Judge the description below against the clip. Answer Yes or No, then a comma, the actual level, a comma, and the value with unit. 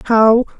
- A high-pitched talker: Yes, high, 225 Hz